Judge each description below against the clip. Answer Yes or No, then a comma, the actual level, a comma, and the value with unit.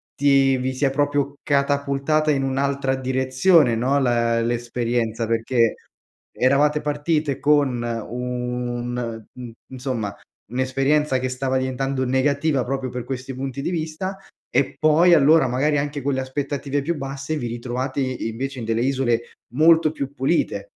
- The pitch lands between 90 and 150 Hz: Yes, low, 135 Hz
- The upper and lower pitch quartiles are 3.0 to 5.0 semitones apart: No, narrow, 2.6 semitones